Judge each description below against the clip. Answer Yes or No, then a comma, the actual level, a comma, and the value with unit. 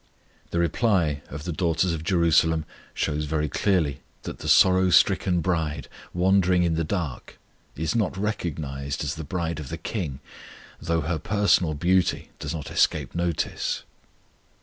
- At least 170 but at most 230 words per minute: No, average, 150 wpm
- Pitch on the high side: No, very low, 85 Hz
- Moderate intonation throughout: Yes, average, 3.2 semitones